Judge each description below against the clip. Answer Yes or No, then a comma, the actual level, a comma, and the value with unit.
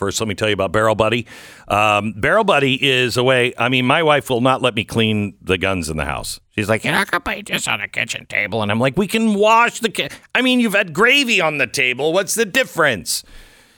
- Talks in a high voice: No, low, 125 Hz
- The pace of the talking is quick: Yes, fast, 255 wpm